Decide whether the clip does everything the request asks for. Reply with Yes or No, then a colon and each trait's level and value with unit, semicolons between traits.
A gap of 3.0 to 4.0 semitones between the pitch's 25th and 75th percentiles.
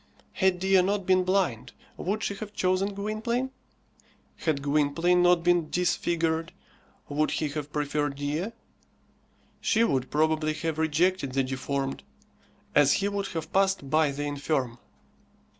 No: average, 4.5 semitones